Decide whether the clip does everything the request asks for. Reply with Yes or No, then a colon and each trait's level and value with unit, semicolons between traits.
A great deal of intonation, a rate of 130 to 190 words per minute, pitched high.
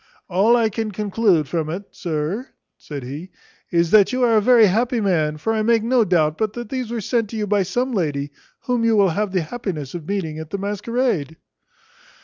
No: wide, 5.9 semitones; average, 200 wpm; high, 200 Hz